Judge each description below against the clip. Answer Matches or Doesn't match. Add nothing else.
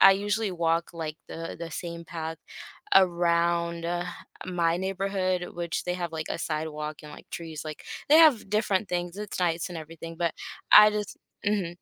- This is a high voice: Doesn't match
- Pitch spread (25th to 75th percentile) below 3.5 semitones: Matches